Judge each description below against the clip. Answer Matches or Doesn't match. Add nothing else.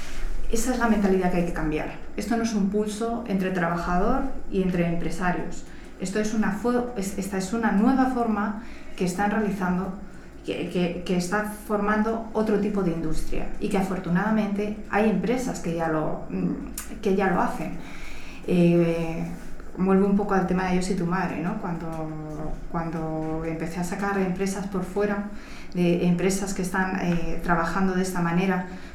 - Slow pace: Doesn't match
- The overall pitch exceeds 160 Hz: Matches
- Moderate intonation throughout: Matches